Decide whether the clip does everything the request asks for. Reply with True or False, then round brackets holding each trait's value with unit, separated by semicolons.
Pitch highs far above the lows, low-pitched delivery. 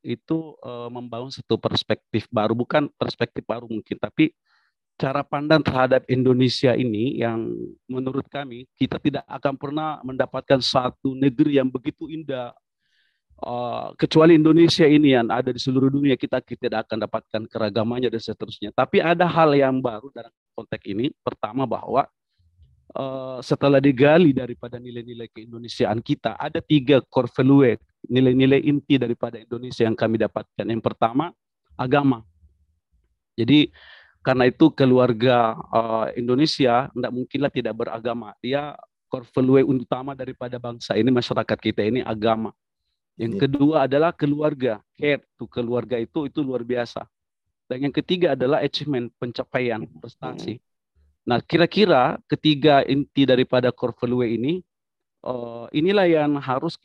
False (3.3 semitones; 125 Hz)